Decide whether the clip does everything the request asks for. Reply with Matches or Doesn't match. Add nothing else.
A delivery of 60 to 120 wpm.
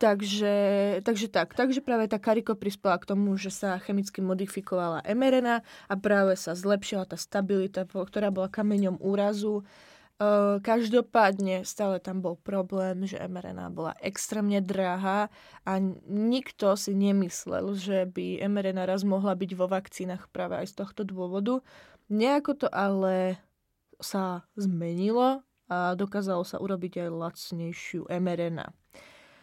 Doesn't match